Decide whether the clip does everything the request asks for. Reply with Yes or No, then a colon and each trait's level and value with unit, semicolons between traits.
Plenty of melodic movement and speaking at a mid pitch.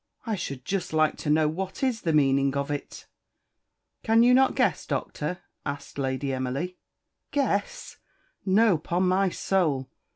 Yes: wide, 5.8 semitones; medium, 165 Hz